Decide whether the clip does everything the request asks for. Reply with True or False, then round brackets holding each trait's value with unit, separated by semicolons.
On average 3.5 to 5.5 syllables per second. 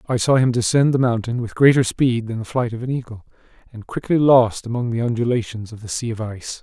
False (6.0 syllables/s)